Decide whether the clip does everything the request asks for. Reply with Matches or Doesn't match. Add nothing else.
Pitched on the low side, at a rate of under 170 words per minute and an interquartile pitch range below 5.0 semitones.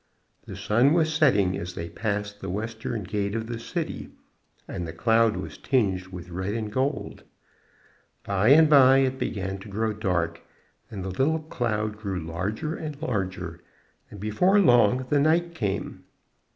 Doesn't match